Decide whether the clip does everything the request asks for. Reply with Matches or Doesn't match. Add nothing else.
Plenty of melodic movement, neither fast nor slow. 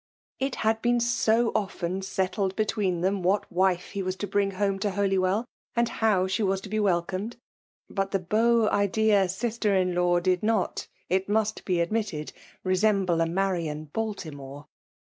Doesn't match